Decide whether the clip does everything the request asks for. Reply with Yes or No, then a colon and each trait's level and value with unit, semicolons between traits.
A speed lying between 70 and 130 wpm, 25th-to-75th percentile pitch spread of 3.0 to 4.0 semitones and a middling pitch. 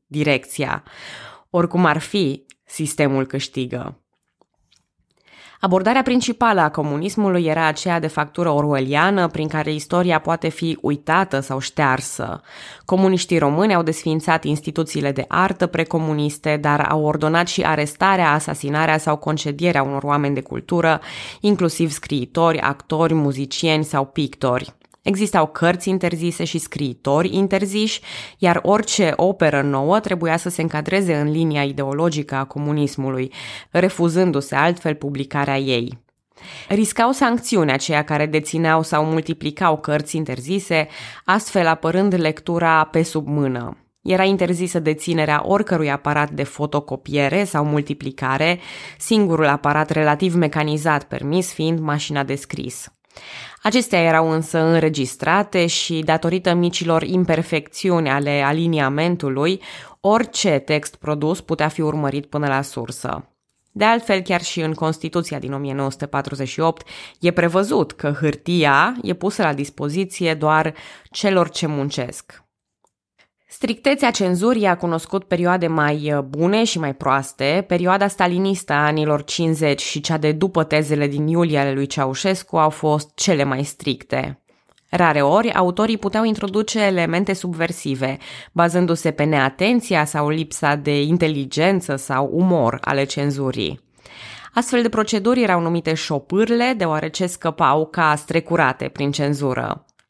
Yes: average, 120 wpm; average, 3.6 semitones; medium, 160 Hz